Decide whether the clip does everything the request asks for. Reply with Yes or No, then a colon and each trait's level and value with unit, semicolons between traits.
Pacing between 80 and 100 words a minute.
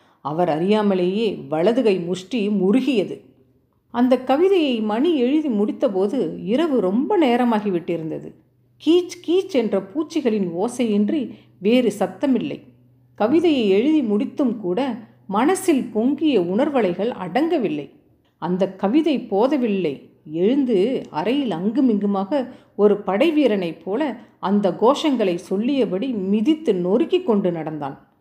Yes: average, 95 wpm